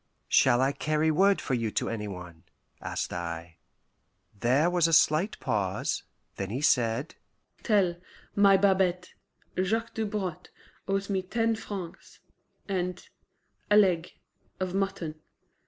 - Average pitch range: No, wide, 8.0 semitones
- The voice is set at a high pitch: No, medium, 175 Hz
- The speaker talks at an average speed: No, slow, 125 wpm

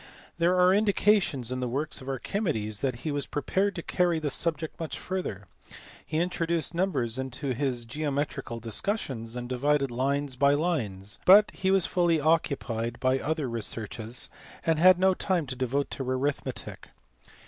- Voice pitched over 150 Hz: No, medium, 145 Hz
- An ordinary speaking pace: Yes, average, 165 wpm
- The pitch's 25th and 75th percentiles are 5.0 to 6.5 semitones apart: Yes, wide, 5.4 semitones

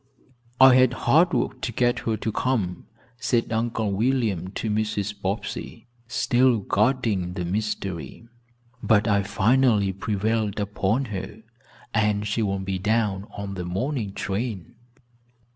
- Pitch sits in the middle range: No, low, 105 Hz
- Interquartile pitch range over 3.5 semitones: No, average, 3.2 semitones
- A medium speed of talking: No, slow, 130 wpm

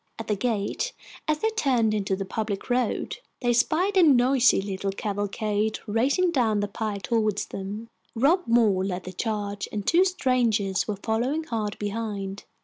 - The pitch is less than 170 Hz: No, high, 220 Hz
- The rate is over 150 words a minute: Yes, average, 160 wpm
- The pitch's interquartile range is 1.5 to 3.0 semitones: No, average, 3.8 semitones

